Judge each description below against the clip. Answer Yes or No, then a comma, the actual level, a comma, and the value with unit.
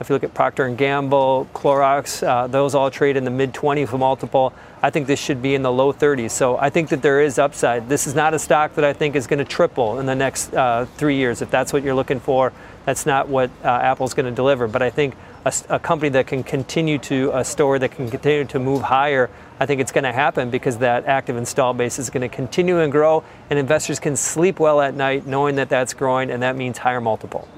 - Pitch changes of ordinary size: No, narrow, 2.1 semitones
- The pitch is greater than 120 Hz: Yes, low, 135 Hz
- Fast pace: Yes, fast, 250 wpm